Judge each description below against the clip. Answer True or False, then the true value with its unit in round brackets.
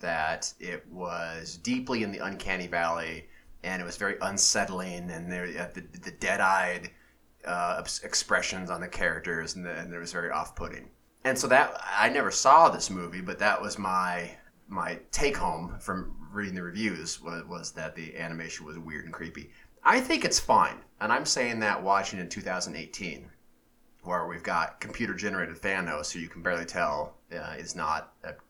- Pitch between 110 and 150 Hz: False (90 Hz)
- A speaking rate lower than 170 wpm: False (175 wpm)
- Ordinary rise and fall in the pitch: False (2.0 semitones)